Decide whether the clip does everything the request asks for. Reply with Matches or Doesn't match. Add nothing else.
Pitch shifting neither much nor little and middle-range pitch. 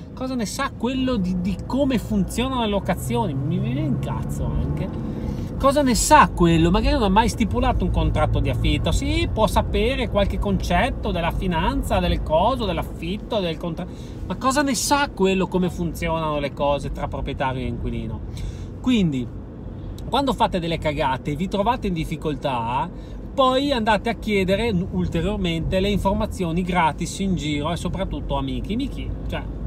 Doesn't match